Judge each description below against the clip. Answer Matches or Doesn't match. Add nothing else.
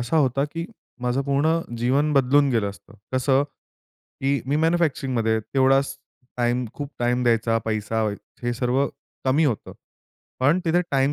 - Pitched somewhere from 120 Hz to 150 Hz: Matches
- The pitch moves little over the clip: Doesn't match